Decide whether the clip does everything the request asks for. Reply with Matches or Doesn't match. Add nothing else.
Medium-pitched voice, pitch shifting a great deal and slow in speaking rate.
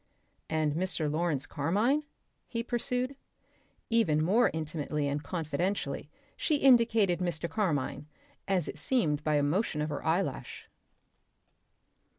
Matches